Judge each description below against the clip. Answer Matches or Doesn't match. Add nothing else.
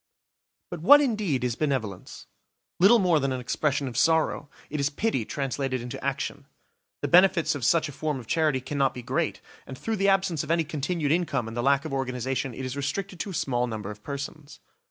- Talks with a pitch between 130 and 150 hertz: Matches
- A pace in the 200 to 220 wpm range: Matches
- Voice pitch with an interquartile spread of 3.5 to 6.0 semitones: Matches